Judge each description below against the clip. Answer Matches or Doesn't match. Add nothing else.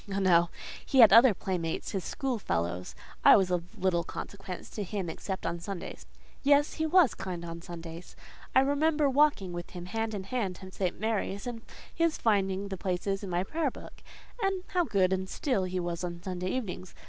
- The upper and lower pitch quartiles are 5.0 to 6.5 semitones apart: Matches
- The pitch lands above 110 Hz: Matches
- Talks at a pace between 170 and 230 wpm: Matches